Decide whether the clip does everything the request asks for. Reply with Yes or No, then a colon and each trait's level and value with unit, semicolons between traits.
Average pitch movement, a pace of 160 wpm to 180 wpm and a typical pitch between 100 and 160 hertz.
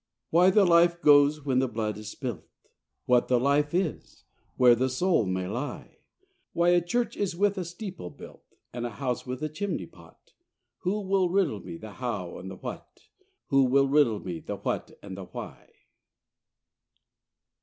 No: wide, 6.9 semitones; average, 175 wpm; medium, 140 Hz